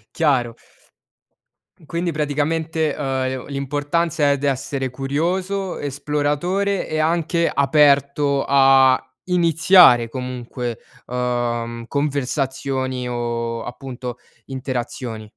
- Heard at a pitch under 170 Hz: Yes, medium, 140 Hz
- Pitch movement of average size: Yes, average, 3.7 semitones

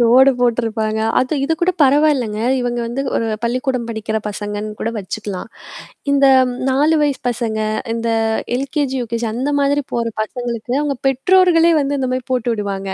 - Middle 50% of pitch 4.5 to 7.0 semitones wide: No, average, 3.7 semitones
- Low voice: No, high, 245 Hz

